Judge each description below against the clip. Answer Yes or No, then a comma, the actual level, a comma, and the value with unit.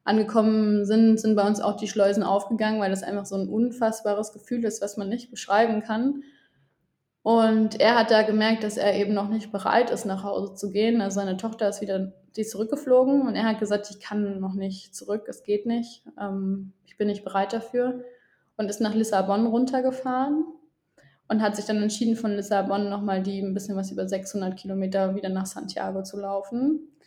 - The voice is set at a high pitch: Yes, high, 210 Hz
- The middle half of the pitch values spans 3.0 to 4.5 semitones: No, narrow, 2.4 semitones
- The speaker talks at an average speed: No, fast, 195 wpm